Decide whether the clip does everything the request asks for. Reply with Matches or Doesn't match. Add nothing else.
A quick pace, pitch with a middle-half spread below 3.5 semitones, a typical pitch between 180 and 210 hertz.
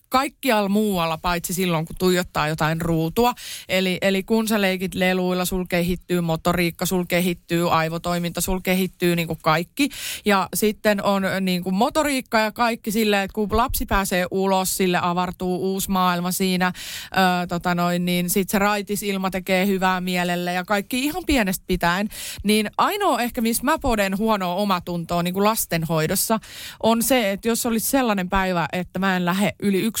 Matches